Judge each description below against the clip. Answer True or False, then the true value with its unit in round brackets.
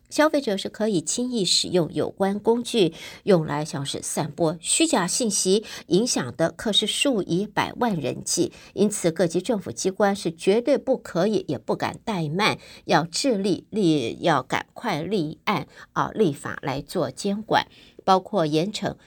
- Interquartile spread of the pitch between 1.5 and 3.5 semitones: False (5.0 semitones)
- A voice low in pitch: False (200 Hz)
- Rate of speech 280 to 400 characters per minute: False (235 characters per minute)